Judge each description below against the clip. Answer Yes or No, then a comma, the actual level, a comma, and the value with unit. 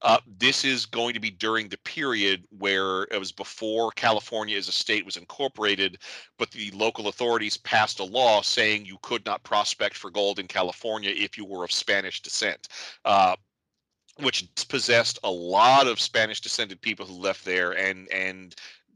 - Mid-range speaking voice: No, low, 105 Hz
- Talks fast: No, average, 175 wpm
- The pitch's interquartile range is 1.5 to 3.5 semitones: Yes, average, 2.8 semitones